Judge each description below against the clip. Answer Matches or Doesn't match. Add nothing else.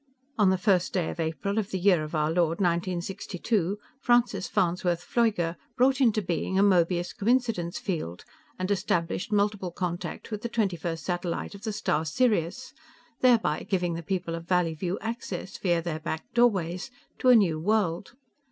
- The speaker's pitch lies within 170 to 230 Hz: Matches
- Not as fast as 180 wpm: Matches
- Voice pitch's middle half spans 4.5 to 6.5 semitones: Doesn't match